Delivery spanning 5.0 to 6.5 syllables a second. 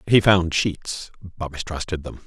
No: 4.4 syllables/s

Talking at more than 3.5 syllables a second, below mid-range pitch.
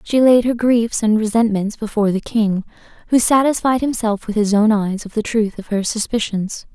No: 5.1 syllables/s; high, 220 Hz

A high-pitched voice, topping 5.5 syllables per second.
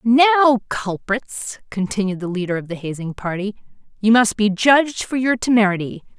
No: high, 215 Hz; 5.2 syllables/s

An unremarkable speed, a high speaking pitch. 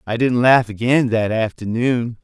No: average, 160 wpm; low, 115 Hz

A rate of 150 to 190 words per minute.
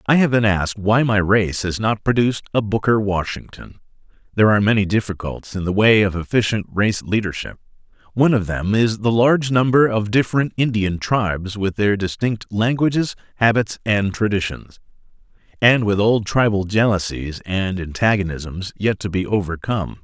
Yes: average, 160 wpm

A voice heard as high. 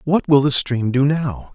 No: medium, 140 Hz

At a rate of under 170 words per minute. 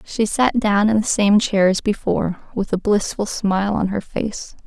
No: fast, 205 wpm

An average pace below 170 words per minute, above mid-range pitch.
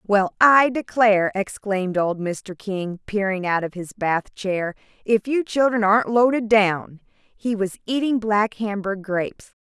Yes: average, 155 wpm; high, 205 Hz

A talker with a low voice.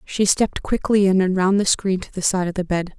No: high, 190 Hz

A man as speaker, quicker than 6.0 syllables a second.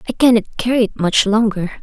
No: female; 6.3 syllables/s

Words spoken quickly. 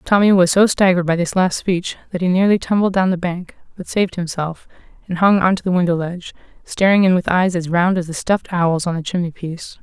Yes: fast, 230 wpm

